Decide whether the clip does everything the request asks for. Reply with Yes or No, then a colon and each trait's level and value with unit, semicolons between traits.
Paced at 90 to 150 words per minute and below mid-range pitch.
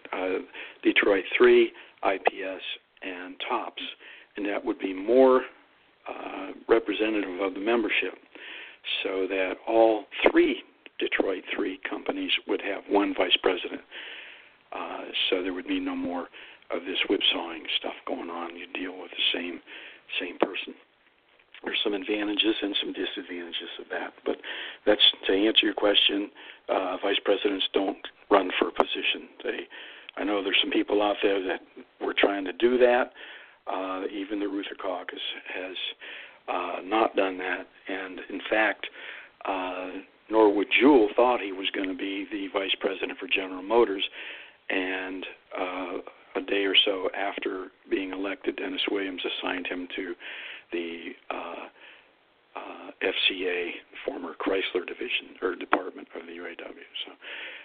Yes: average, 145 wpm; low, 110 Hz